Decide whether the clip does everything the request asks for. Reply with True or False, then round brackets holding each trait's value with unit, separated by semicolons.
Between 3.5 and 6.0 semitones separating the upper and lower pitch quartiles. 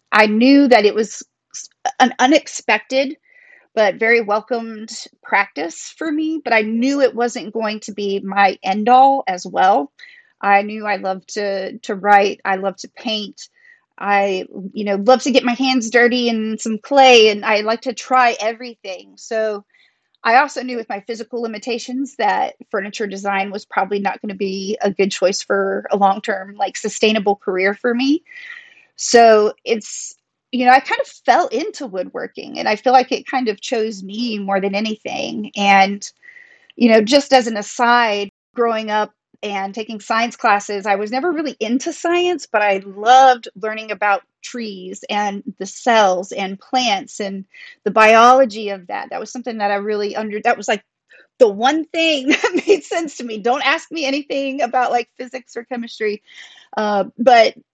True (4.1 semitones)